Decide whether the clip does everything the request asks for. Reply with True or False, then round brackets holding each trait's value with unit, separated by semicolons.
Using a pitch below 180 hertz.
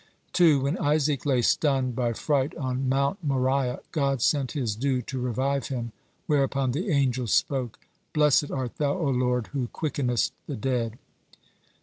True (135 Hz)